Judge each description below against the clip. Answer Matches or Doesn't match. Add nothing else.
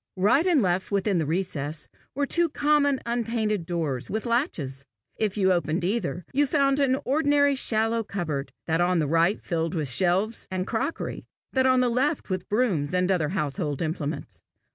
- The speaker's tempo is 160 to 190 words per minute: Matches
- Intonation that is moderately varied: Doesn't match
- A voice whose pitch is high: Matches